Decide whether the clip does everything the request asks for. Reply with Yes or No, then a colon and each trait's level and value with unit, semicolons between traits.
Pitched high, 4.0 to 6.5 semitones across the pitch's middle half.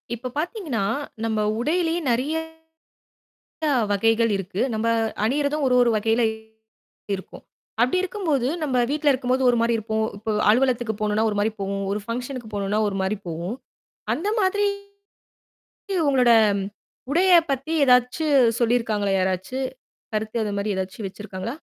Yes: high, 235 Hz; average, 4.6 semitones